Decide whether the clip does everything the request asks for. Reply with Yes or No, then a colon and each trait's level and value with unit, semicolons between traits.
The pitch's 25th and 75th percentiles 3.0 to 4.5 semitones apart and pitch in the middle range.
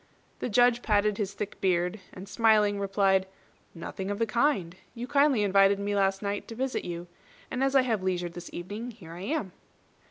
No: average, 3.5 semitones; high, 205 Hz